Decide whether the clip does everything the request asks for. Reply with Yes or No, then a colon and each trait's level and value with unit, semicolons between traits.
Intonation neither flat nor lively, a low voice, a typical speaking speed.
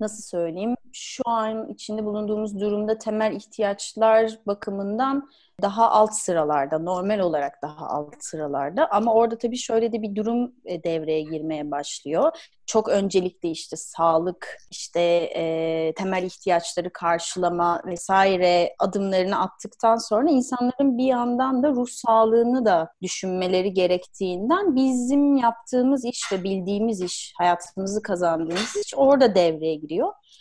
No: average, 4.8 semitones; high, 205 Hz; average, 120 wpm